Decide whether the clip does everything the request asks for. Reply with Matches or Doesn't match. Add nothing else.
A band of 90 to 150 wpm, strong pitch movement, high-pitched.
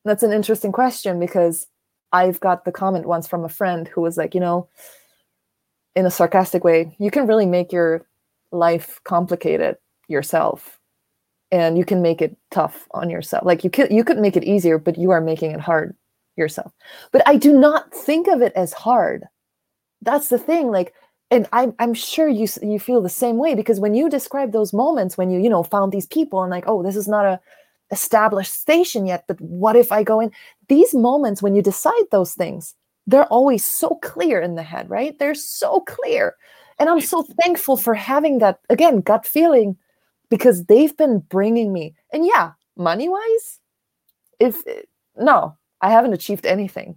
Doesn't match